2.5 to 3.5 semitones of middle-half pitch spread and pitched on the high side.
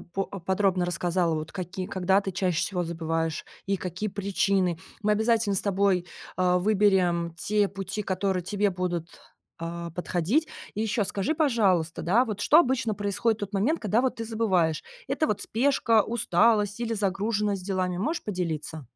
Yes: average, 3.2 semitones; high, 195 Hz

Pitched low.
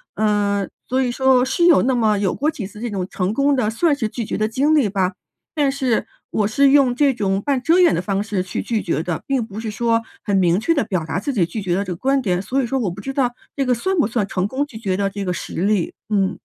No: high, 220 Hz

